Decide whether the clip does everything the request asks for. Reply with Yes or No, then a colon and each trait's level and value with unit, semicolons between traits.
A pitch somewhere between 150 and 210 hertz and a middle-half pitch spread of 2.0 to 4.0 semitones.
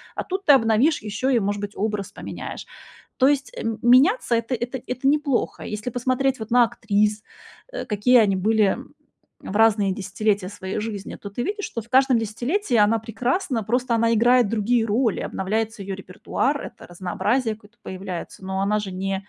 No: high, 225 Hz; average, 3.6 semitones